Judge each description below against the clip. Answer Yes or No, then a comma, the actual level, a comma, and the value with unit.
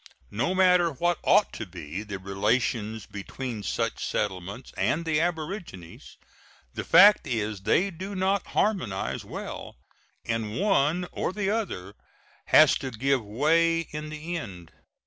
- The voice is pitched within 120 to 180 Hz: Yes, medium, 140 Hz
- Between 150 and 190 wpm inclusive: No, slow, 135 wpm